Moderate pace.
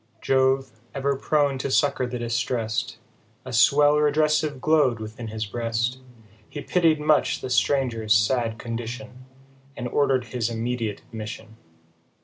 No: slow, 130 wpm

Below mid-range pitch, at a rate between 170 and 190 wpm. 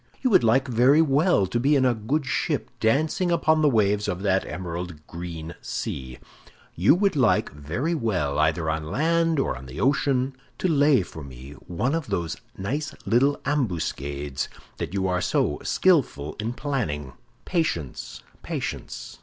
No: low, 110 Hz; average, 155 wpm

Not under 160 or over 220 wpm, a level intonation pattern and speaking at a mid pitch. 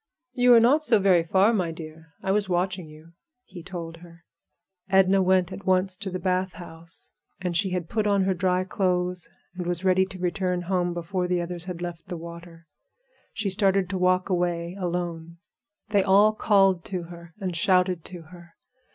Yes: average, 185 wpm; narrow, 1.9 semitones; medium, 180 Hz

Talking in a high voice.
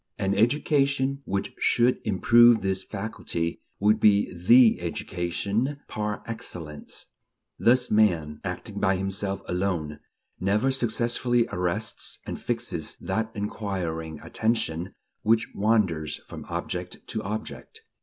No: low, 105 Hz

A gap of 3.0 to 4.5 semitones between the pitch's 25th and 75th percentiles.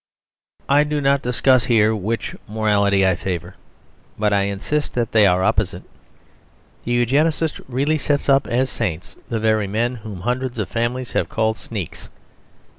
Yes: average, 3.9 semitones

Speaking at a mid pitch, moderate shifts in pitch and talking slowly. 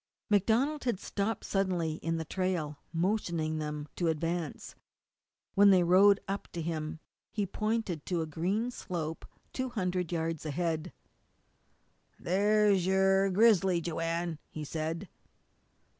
Yes: medium, 180 Hz; average, 3.6 semitones; slow, 125 wpm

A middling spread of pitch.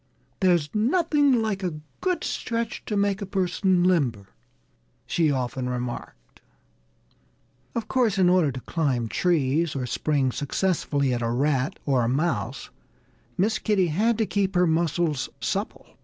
No: wide, 7.0 semitones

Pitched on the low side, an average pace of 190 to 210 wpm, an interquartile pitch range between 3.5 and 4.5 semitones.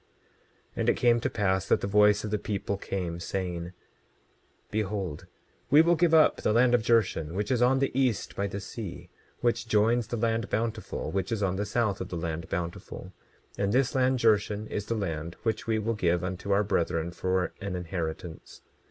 Yes: low, 105 Hz; average, 195 wpm; average, 4.1 semitones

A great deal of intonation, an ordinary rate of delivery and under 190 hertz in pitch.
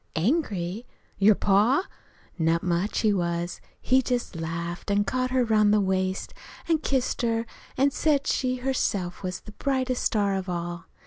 No: wide, 6.1 semitones; average, 155 wpm; high, 205 Hz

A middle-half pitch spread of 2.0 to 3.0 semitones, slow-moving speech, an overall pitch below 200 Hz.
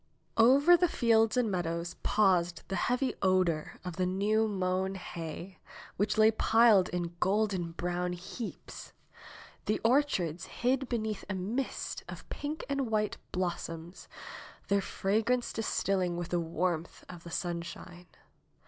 No: average, 4.1 semitones; slow, 130 wpm; high, 190 Hz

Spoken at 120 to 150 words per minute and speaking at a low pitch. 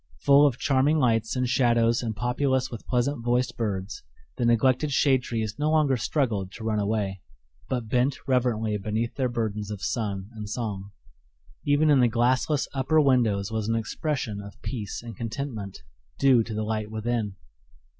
No: average, 165 wpm; low, 120 Hz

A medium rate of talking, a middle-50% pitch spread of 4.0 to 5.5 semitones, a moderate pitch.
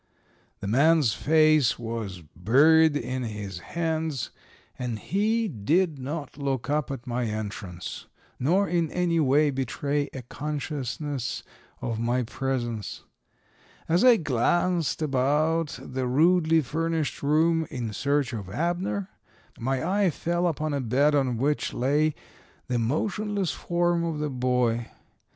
No: slow, 130 wpm; average, 4.7 semitones; medium, 145 Hz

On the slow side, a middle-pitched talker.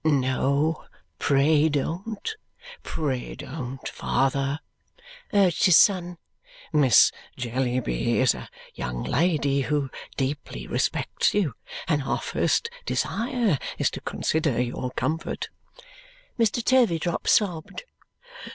Yes: slow, 100 wpm; medium, 150 Hz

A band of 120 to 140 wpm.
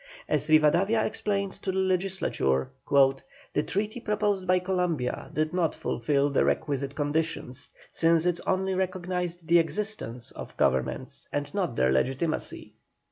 Yes: slow, 135 wpm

